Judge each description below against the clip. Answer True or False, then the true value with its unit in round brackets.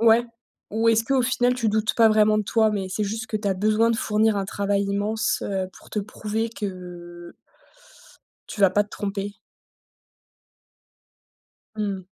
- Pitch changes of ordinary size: False (2.0 semitones)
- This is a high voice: True (210 Hz)